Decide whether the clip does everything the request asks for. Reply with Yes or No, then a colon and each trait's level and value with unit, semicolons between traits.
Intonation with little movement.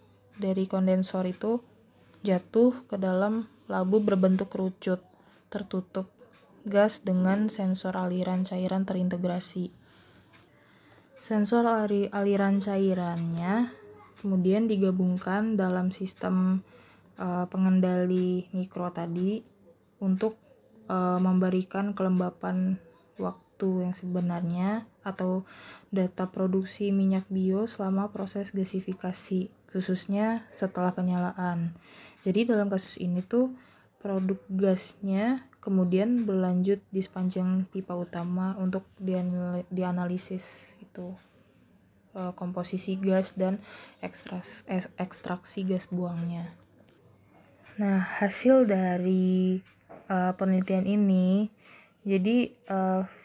Yes: narrow, 1.5 semitones